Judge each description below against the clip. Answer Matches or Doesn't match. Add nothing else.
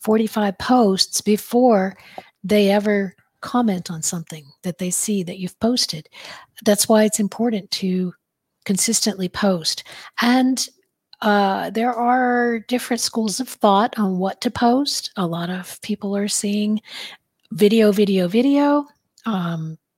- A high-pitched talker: Matches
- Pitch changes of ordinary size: Matches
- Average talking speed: Doesn't match